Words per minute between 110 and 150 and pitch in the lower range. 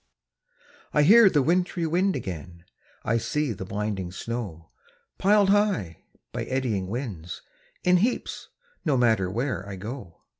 Yes: slow, 135 wpm; low, 120 Hz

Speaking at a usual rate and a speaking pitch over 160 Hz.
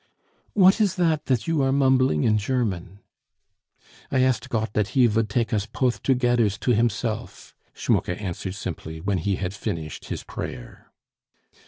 No: average, 155 wpm; low, 115 Hz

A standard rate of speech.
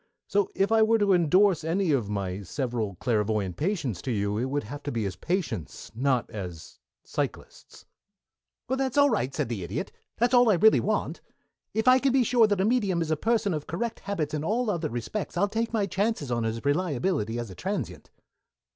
No: fast, 210 wpm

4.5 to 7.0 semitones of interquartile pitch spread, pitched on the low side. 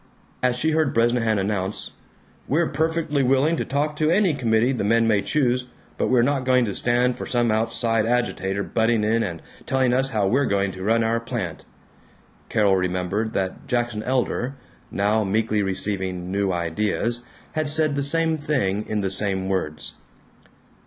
Yes: average, 4.8 semitones; low, 115 Hz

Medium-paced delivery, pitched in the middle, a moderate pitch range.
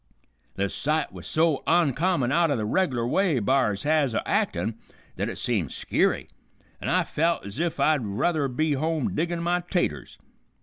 No: average, 170 wpm; medium, 150 Hz; wide, 6.0 semitones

